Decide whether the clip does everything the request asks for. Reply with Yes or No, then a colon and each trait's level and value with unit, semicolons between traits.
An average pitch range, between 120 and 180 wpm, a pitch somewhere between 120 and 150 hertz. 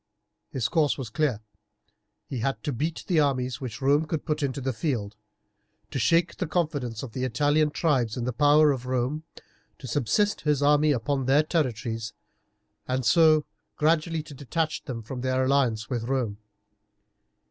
Yes: average, 3.7 semitones; average, 165 wpm; low, 135 Hz